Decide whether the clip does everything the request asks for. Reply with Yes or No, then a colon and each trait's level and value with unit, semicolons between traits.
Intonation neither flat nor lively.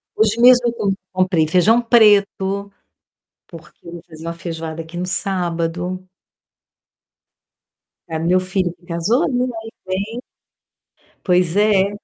Yes: average, 3.8 semitones